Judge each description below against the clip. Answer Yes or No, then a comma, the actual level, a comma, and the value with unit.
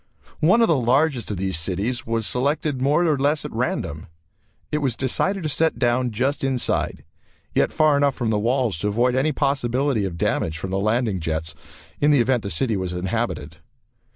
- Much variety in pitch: Yes, wide, 5.9 semitones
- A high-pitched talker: No, low, 125 Hz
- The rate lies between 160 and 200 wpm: Yes, average, 190 wpm